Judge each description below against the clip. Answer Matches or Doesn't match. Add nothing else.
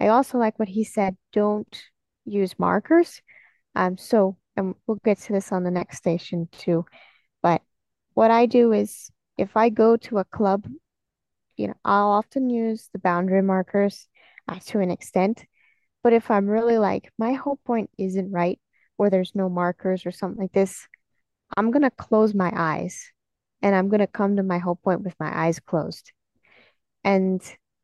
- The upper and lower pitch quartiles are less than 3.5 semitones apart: Matches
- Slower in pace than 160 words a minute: Doesn't match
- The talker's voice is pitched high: Matches